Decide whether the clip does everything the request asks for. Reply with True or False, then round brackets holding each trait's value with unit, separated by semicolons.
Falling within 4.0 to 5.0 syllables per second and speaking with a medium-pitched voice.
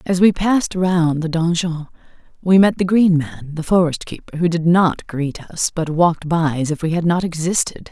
True (4.9 syllables/s; 170 Hz)